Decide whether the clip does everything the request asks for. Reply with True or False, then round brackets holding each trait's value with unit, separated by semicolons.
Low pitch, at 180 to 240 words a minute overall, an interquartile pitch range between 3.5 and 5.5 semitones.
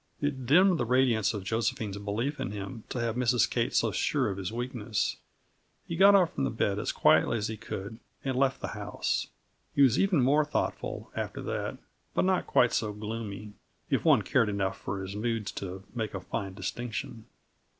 True (115 Hz; 190 wpm; 4.3 semitones)